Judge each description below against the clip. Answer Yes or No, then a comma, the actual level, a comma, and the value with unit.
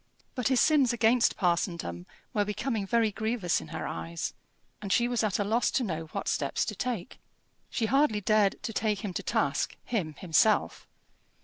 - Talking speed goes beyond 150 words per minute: Yes, average, 180 wpm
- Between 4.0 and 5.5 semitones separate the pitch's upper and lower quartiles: Yes, average, 4.8 semitones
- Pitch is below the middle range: No, high, 215 Hz